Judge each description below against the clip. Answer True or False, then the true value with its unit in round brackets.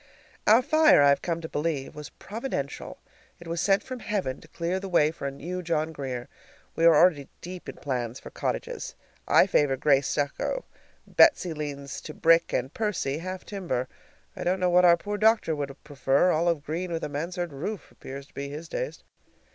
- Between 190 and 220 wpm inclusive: True (195 wpm)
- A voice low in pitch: False (165 Hz)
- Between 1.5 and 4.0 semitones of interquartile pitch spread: False (4.5 semitones)